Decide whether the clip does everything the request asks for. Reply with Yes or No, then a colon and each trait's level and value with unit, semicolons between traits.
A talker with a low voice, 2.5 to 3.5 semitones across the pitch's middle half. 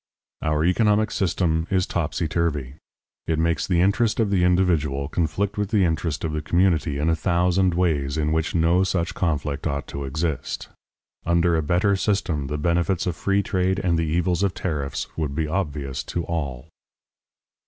Yes: very low, 85 Hz; average, 3.2 semitones